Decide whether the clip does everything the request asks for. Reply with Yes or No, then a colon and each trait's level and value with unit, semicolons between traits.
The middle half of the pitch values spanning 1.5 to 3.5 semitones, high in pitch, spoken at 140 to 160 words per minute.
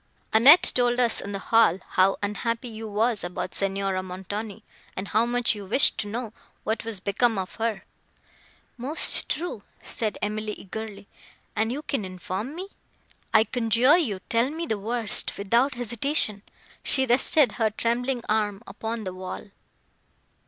Yes: average, 3.2 semitones; high, 220 Hz; average, 150 wpm